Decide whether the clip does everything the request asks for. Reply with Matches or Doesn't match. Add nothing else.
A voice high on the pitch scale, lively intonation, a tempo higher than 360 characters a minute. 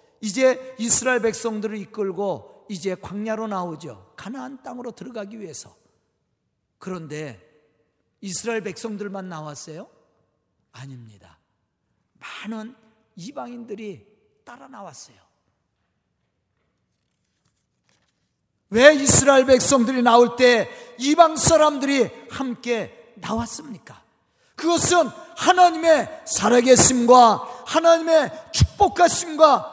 Doesn't match